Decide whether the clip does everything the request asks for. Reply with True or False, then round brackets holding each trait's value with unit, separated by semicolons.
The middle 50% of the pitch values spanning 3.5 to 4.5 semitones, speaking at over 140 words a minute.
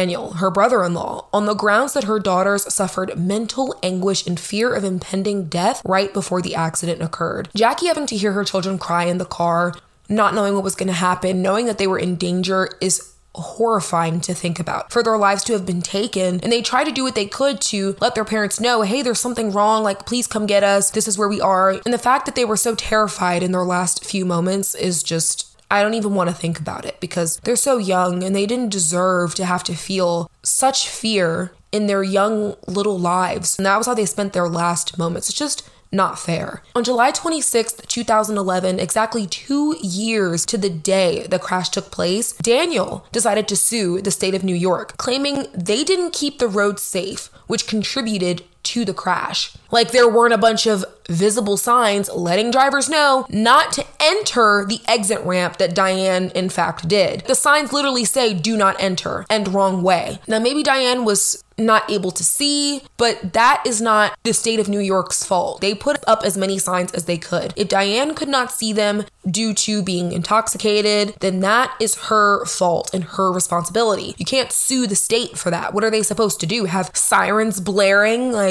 True (3.8 semitones; 205 wpm)